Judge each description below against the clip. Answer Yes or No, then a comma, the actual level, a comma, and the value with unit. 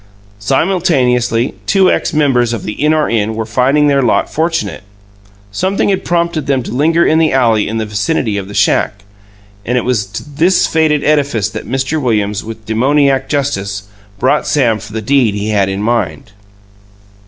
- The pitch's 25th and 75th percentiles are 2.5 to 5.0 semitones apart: No, wide, 5.5 semitones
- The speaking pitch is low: Yes, low, 125 Hz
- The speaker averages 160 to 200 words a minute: Yes, average, 175 wpm